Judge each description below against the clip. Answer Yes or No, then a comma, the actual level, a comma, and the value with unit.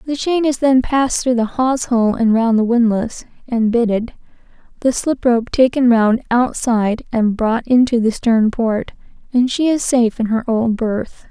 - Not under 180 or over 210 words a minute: Yes, average, 185 wpm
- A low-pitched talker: No, high, 235 Hz